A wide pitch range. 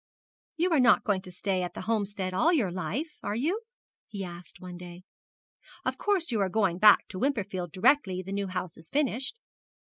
Yes: wide, 6.0 semitones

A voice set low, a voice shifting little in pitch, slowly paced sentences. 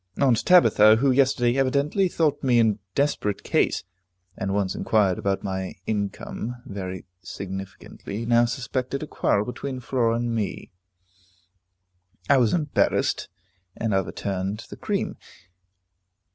No: low, 115 Hz; average, 5.1 semitones; slow, 120 wpm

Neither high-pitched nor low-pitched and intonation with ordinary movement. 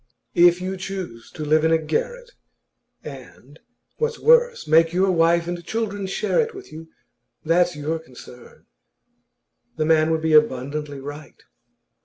Yes: medium, 165 Hz; average, 3.8 semitones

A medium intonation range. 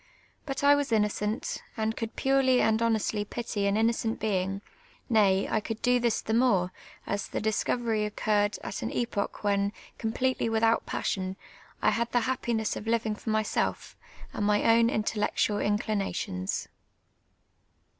No: narrow, 2.0 semitones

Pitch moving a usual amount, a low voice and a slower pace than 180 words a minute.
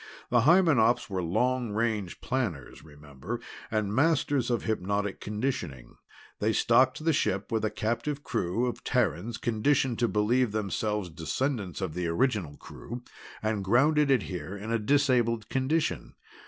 Yes: average, 4.6 semitones; low, 110 Hz; average, 140 wpm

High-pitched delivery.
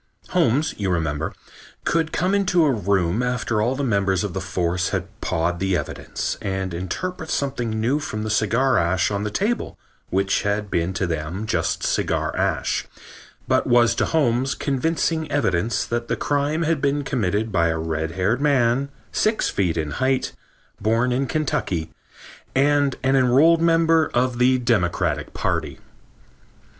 No: low, 120 Hz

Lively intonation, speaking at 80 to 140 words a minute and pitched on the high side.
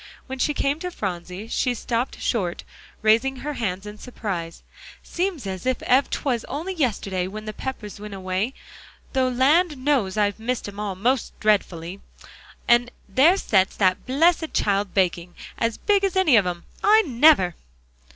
No: wide, 6.0 semitones; average, 160 wpm; high, 230 Hz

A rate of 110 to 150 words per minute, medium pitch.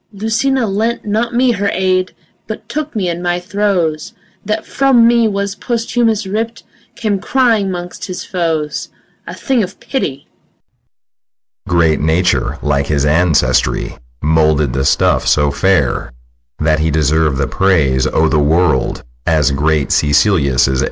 Yes: average, 145 wpm; medium, 160 Hz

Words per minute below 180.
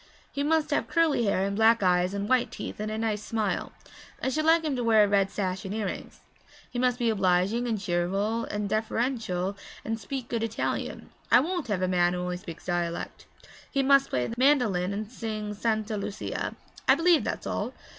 No: average, 200 wpm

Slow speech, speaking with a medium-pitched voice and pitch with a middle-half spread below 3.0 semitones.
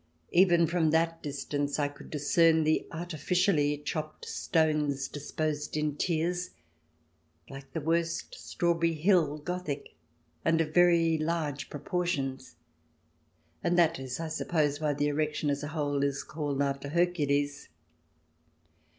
Yes: slow, 130 wpm; medium, 155 Hz; narrow, 2.6 semitones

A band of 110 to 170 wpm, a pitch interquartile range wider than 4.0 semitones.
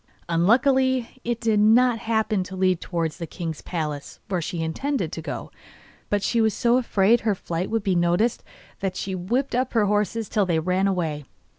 No: average, 185 wpm; average, 4.8 semitones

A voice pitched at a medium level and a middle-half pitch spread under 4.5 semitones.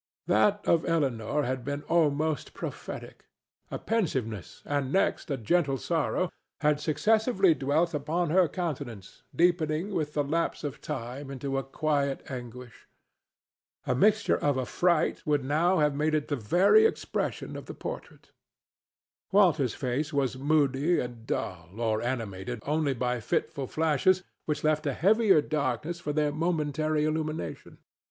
Yes: medium, 150 Hz; average, 4.0 semitones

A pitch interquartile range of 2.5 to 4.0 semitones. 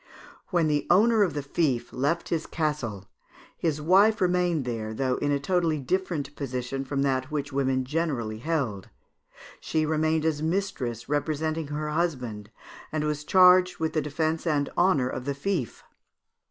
Yes: average, 3.7 semitones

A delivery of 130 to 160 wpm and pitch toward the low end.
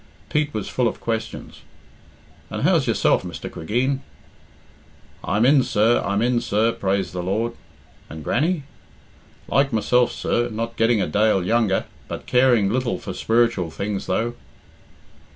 Yes: average, 140 wpm; low, 115 Hz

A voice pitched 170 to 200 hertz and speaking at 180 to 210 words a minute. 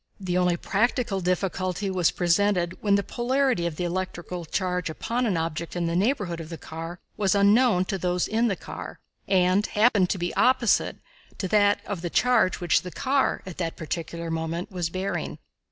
Yes: medium, 185 Hz; average, 185 wpm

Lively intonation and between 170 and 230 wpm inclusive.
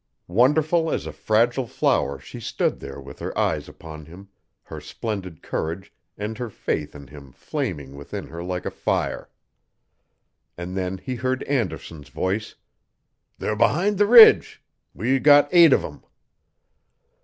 No: wide, 8.5 semitones; average, 145 wpm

